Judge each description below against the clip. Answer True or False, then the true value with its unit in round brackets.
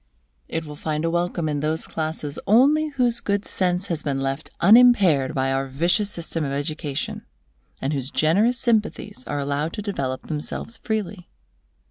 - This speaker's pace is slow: False (160 wpm)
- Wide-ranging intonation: True (6.1 semitones)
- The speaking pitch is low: False (165 Hz)